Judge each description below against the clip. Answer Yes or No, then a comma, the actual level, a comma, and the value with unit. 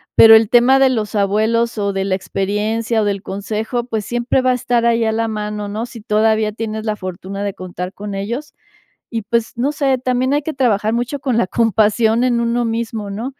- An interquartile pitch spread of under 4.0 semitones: Yes, narrow, 2.5 semitones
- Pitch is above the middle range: Yes, high, 225 Hz